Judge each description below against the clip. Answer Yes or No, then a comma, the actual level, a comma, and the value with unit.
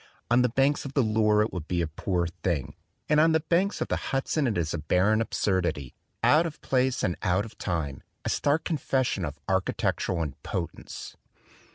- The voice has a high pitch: No, low, 105 Hz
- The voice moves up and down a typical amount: No, wide, 7.7 semitones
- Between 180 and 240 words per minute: Yes, average, 190 wpm